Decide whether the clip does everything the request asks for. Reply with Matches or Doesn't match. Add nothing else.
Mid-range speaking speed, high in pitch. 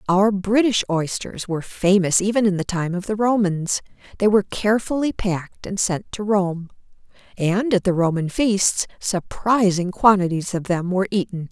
Matches